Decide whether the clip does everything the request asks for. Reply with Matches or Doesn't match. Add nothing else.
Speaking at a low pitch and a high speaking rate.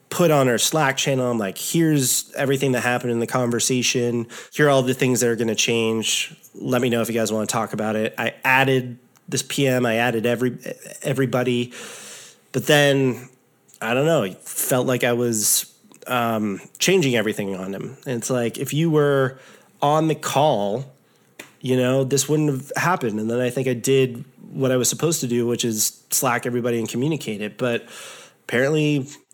Doesn't match